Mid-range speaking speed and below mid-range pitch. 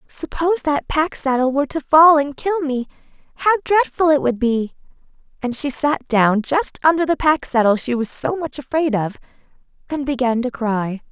No: average, 185 wpm; very high, 275 Hz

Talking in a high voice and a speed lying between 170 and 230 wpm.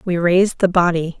No: medium, 175 Hz; average, 200 wpm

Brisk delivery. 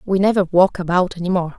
Yes: fast, 225 wpm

